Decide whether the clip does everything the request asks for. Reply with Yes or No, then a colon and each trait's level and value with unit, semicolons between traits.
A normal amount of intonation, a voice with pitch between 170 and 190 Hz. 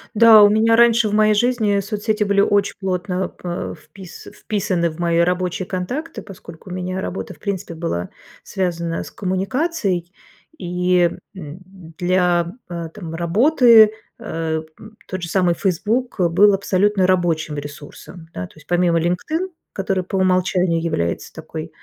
Yes: average, 3.3 semitones; medium, 185 Hz